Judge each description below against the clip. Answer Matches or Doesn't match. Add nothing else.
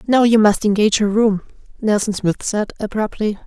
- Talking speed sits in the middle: Matches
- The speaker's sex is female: Matches